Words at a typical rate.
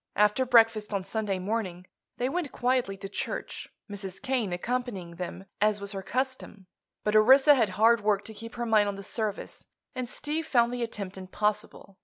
Yes: average, 180 wpm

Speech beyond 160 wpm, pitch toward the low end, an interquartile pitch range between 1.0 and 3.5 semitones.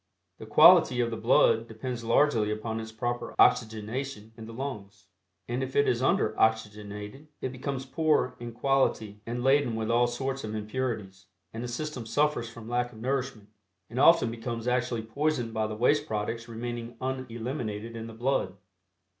Yes: average, 170 wpm; low, 120 Hz; average, 2.8 semitones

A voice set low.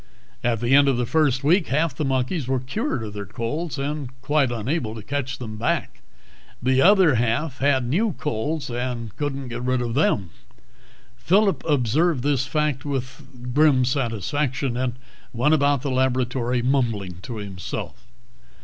Yes: low, 130 Hz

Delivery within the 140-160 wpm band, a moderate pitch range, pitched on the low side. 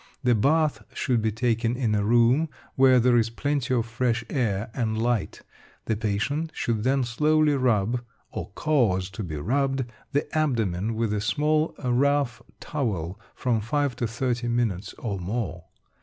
Yes: average, 155 wpm; average, 3.8 semitones; low, 120 Hz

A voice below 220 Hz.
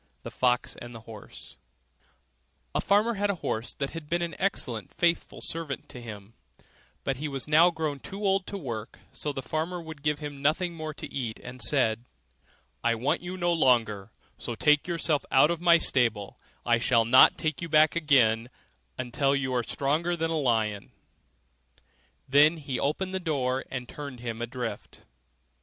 Yes: medium, 140 Hz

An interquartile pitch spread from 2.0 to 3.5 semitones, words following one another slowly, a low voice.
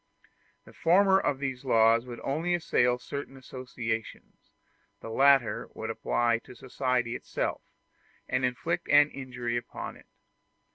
Yes: average, 2.8 semitones; slow, 130 wpm; low, 130 Hz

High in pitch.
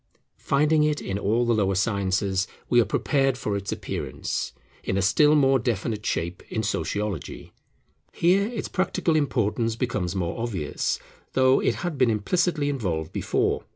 No: low, 115 Hz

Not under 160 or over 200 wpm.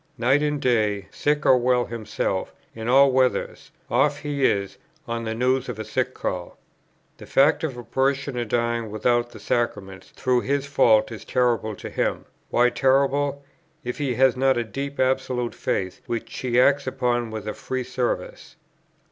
Yes: average, 170 wpm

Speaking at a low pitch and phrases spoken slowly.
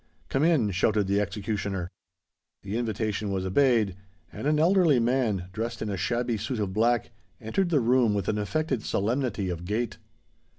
No: low, 110 Hz; average, 165 wpm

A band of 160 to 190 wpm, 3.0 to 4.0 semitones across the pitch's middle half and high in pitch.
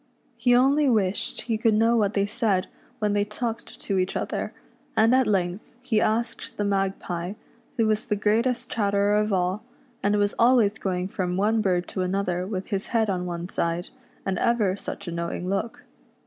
Yes: average, 185 wpm; average, 3.3 semitones; high, 205 Hz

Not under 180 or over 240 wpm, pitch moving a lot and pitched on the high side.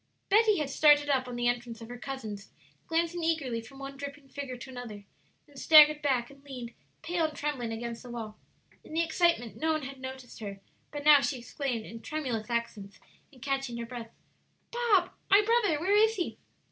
No: average, 195 wpm; average, 4.6 semitones; very high, 275 Hz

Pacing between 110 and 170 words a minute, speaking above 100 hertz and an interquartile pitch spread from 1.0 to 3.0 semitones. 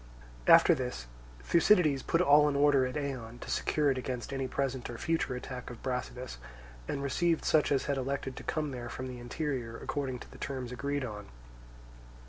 No: average, 185 wpm; low, 135 Hz; narrow, 2.5 semitones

